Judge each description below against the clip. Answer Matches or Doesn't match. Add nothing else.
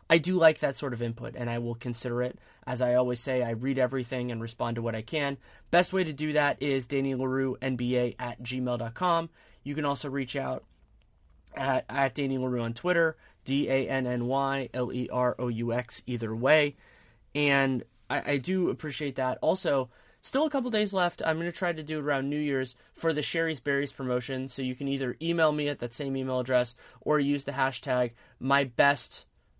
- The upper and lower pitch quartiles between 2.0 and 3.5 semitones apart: Matches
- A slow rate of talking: Doesn't match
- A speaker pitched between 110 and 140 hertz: Matches